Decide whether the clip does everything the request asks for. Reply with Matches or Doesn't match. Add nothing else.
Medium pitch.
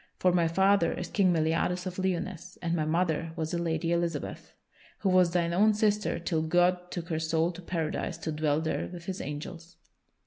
Matches